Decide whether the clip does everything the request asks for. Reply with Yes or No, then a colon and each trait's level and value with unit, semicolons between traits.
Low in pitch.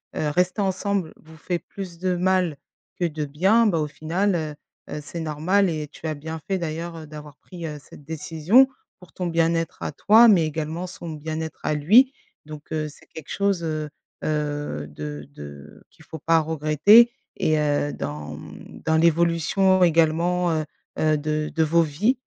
No: medium, 160 Hz